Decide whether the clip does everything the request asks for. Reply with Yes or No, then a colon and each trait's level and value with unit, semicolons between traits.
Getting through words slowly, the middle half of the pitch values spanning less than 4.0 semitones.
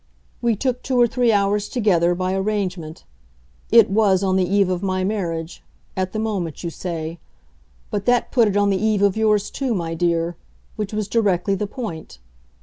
No: average, 185 wpm; average, 3.3 semitones